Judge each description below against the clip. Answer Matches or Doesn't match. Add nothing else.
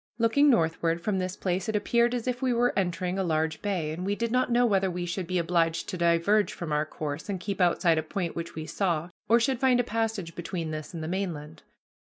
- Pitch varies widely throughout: Doesn't match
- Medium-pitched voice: Matches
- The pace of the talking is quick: Matches